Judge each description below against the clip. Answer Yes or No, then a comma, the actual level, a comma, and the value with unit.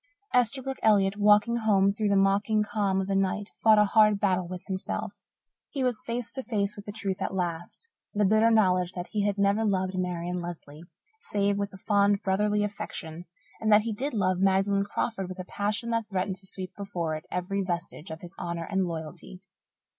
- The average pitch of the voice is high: Yes, high, 200 Hz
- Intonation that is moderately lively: No, narrow, 2.3 semitones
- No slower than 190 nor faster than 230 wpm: Yes, average, 200 wpm